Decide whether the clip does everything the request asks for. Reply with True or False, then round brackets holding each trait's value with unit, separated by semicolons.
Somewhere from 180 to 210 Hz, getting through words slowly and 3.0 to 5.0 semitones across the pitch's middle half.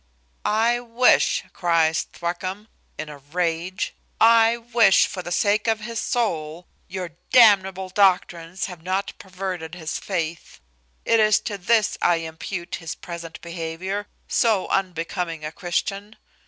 True (185 Hz; 130 wpm; 3.9 semitones)